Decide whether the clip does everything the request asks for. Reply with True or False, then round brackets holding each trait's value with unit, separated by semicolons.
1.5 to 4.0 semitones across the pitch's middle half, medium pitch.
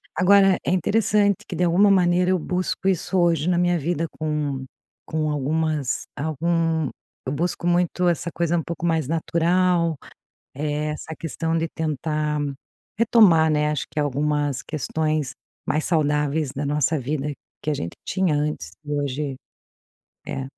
True (2.9 semitones; 160 Hz)